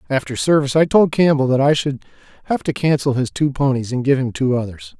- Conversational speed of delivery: No, fast, 230 wpm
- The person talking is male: Yes, male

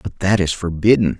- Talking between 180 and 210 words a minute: Yes, average, 200 wpm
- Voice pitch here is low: Yes, very low, 90 Hz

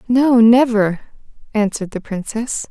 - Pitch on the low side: No, high, 225 Hz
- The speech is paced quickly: No, slow, 110 wpm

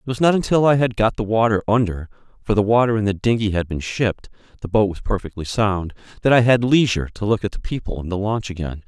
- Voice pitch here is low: Yes, low, 105 Hz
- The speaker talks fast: Yes, fast, 250 wpm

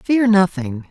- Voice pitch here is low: No, high, 190 Hz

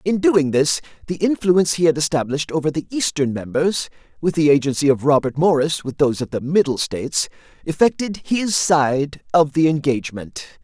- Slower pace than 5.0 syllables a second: No, 5.4 syllables/s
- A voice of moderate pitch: Yes, medium, 155 Hz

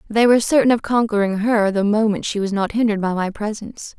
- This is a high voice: Yes, high, 215 Hz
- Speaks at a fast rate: Yes, fast, 225 wpm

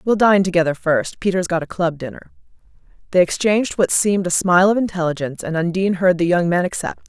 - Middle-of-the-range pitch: Yes, medium, 180 Hz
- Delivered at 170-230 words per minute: Yes, average, 195 wpm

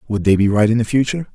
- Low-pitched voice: Yes, low, 115 Hz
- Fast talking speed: Yes, fast, 310 wpm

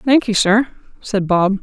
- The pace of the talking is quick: No, average, 145 wpm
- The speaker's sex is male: No, female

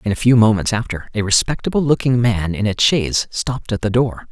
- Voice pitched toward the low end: Yes, low, 115 Hz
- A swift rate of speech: Yes, fast, 225 wpm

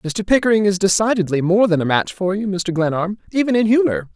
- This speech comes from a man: Yes, male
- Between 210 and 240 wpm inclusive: Yes, fast, 215 wpm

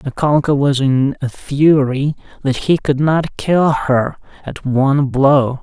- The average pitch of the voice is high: No, medium, 140 Hz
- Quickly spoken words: No, average, 150 wpm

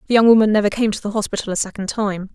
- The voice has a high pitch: Yes, high, 210 Hz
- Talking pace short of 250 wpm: No, fast, 280 wpm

